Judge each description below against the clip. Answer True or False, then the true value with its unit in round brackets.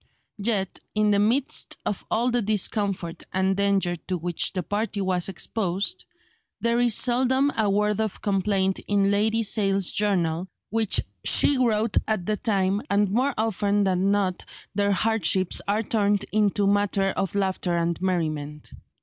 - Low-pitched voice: False (200 Hz)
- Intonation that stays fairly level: True (2.3 semitones)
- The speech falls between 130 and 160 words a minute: True (150 wpm)